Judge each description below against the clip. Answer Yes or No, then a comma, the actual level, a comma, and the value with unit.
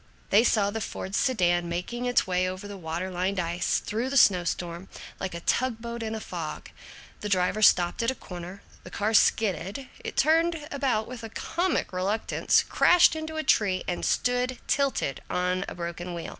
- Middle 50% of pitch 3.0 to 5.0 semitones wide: No, wide, 5.5 semitones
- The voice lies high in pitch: Yes, high, 205 Hz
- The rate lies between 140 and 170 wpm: No, average, 185 wpm